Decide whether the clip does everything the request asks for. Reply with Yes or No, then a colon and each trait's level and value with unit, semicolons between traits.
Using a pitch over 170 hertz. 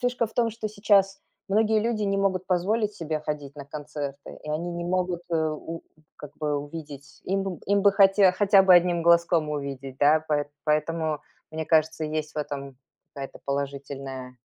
No: medium, 165 Hz